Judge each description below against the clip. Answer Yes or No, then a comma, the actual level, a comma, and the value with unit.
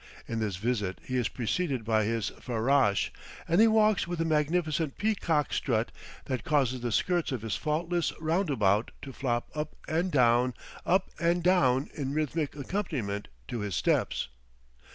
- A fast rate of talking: No, average, 155 wpm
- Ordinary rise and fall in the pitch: No, wide, 6.2 semitones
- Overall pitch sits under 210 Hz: Yes, medium, 140 Hz